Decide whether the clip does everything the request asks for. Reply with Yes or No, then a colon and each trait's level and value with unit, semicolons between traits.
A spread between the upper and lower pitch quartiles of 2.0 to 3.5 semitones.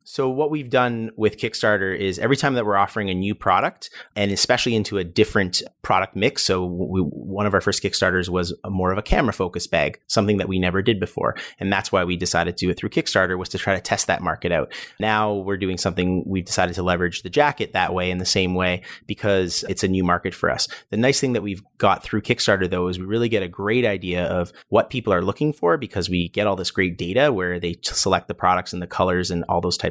Yes: narrow, 2.6 semitones